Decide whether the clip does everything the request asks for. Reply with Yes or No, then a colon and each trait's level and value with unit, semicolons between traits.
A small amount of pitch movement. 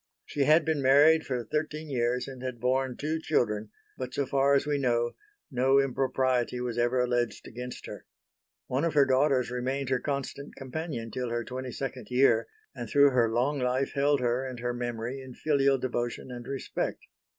Yes: narrow, 2.2 semitones